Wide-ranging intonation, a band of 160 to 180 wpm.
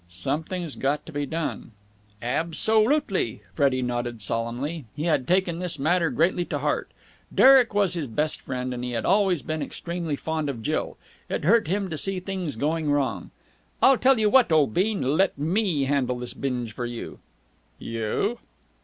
Yes: wide, 6.4 semitones; average, 170 wpm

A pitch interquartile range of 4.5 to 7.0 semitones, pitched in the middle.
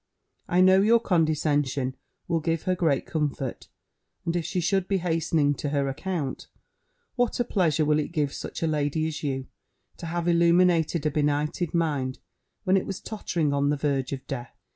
No: average, 3.3 semitones; medium, 160 Hz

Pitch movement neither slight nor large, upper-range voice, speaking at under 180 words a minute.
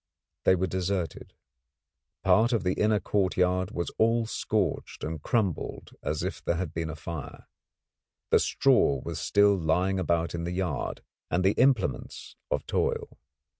No: average, 3.5 semitones; very low, 90 Hz; average, 150 wpm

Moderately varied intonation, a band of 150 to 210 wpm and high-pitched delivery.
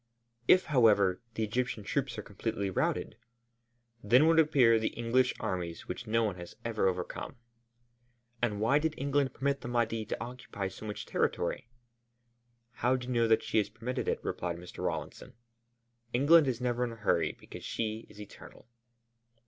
No: average, 3.4 semitones; average, 165 wpm; low, 115 Hz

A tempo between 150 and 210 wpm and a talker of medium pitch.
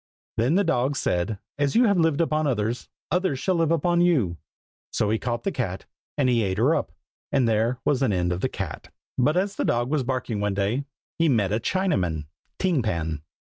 No: fast, 205 wpm; low, 125 Hz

